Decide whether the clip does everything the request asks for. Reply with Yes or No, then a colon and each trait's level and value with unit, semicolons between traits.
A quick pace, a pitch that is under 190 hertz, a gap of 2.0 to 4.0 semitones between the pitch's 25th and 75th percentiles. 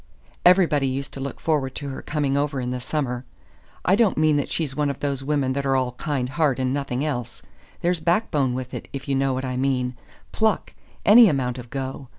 Yes: fast, 215 wpm; low, 135 Hz; narrow, 2.6 semitones